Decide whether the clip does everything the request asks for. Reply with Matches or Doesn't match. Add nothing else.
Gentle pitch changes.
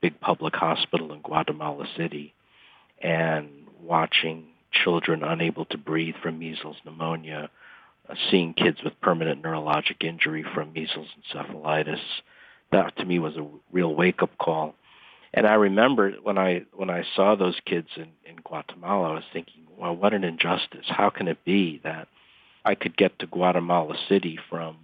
Matches